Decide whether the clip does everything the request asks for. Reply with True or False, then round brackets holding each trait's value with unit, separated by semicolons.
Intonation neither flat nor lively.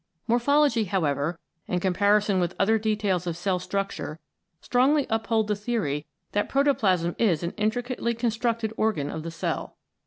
True (4.5 semitones)